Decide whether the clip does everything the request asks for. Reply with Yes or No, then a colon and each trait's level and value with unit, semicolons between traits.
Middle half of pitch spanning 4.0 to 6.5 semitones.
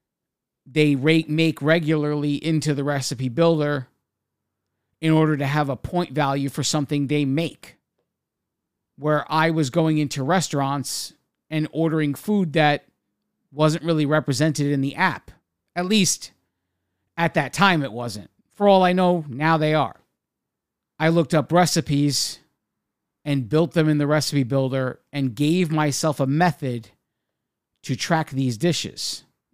No: average, 2.7 semitones